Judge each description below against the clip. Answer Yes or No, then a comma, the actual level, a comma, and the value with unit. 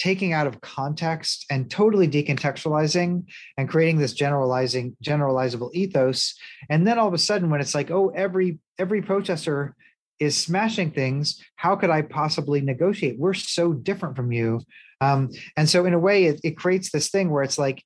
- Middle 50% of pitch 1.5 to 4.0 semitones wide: No, average, 4.8 semitones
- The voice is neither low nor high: Yes, medium, 155 Hz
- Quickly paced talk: No, average, 180 wpm